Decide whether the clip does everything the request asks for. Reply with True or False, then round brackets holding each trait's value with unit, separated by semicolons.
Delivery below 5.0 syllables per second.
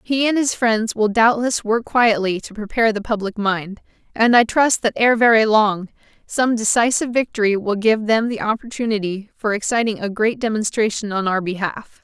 False (5.1 syllables/s)